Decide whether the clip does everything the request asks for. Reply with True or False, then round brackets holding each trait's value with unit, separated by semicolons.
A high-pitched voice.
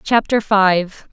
True (200 Hz)